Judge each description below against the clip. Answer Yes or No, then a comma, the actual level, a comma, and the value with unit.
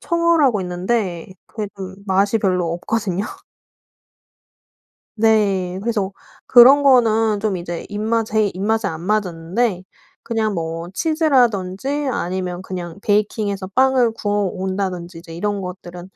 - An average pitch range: Yes, average, 3.7 semitones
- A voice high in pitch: Yes, high, 200 Hz